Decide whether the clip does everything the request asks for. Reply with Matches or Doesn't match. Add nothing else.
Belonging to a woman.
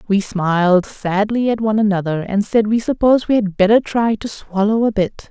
Matches